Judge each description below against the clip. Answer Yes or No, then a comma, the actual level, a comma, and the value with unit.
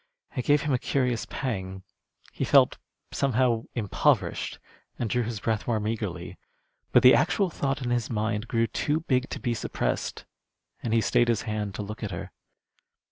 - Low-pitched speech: Yes, low, 115 Hz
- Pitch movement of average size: Yes, average, 3.0 semitones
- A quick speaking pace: No, average, 175 wpm